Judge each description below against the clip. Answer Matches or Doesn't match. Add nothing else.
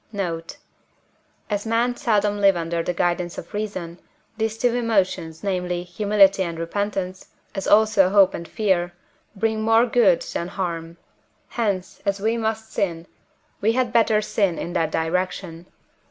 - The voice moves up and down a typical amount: Matches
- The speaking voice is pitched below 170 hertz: Doesn't match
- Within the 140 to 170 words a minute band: Matches